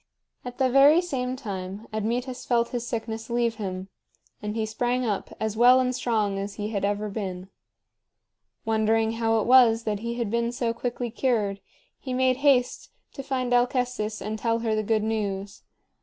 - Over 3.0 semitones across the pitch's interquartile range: No, average, 2.7 semitones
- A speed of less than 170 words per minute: No, average, 175 wpm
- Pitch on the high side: Yes, high, 230 Hz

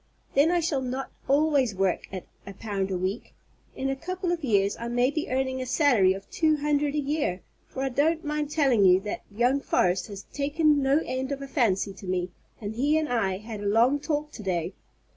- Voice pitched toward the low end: No, very high, 260 Hz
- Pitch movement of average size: No, wide, 6.5 semitones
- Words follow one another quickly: Yes, fast, 220 wpm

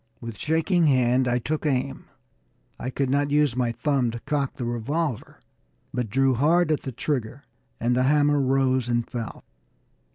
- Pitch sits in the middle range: No, low, 130 Hz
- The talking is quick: No, average, 165 wpm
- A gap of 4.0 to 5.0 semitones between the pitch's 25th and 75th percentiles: No, average, 3.2 semitones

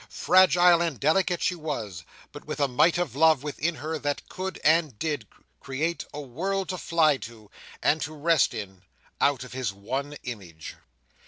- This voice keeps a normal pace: Yes, average, 170 wpm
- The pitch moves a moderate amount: Yes, average, 4.9 semitones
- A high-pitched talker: No, medium, 150 Hz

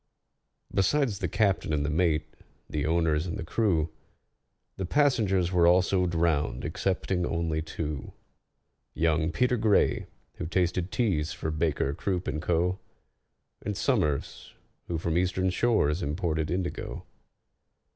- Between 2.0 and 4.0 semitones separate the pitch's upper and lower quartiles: Yes, average, 3.3 semitones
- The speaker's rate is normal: No, slow, 125 wpm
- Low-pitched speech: Yes, very low, 85 Hz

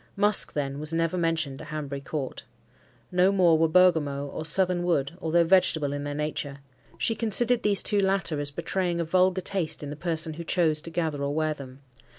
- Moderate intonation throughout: Yes, average, 3.8 semitones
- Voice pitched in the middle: Yes, medium, 165 Hz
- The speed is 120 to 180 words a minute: No, average, 195 wpm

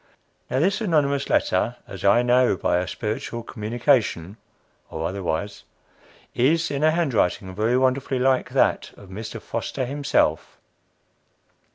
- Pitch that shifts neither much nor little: No, wide, 5.7 semitones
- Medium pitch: No, low, 120 Hz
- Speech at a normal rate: No, slow, 130 wpm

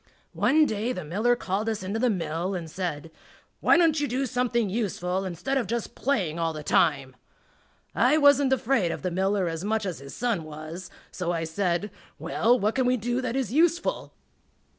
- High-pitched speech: Yes, high, 205 Hz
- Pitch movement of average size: No, wide, 6.4 semitones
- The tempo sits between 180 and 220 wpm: Yes, average, 190 wpm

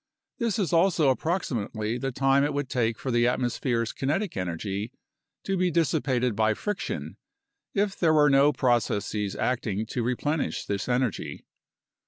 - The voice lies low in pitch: Yes, low, 130 Hz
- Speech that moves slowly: No, average, 150 wpm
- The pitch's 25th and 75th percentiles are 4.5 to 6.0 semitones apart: Yes, wide, 5.4 semitones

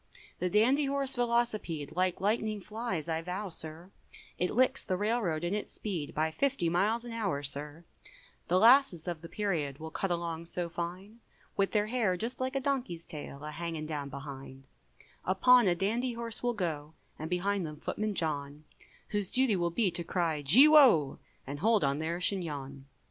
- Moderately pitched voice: Yes, medium, 180 Hz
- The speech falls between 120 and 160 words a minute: No, average, 180 wpm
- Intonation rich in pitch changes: Yes, wide, 5.9 semitones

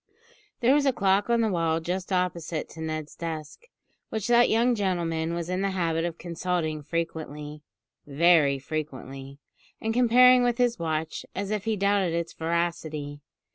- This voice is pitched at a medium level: Yes, medium, 170 Hz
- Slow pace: No, average, 160 wpm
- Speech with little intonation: No, average, 4.3 semitones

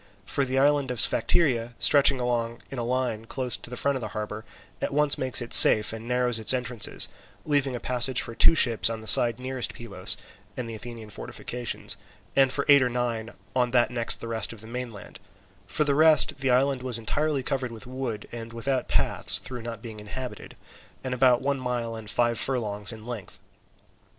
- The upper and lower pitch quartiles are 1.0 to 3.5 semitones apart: Yes, narrow, 2.4 semitones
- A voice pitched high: No, low, 125 Hz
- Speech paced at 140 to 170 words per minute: No, average, 195 wpm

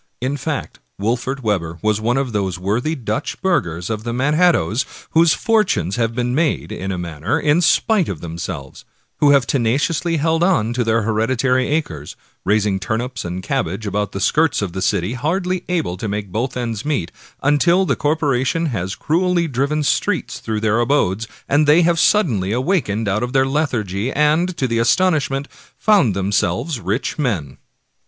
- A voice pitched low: Yes, low, 125 Hz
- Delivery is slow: No, average, 170 wpm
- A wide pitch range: Yes, wide, 6.8 semitones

